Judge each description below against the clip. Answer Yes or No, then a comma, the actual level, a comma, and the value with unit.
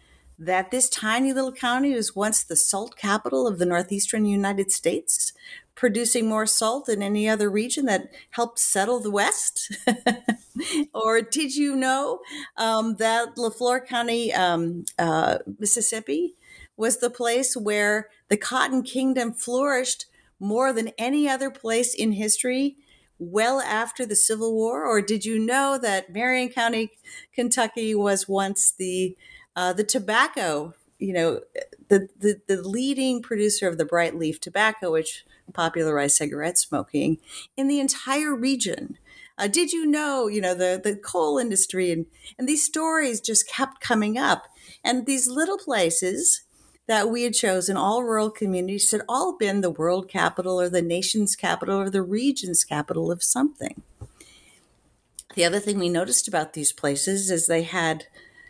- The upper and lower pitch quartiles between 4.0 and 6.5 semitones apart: Yes, average, 5.0 semitones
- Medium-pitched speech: No, high, 220 Hz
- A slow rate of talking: No, average, 150 wpm